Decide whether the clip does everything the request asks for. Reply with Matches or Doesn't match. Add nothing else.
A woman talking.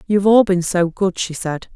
Matches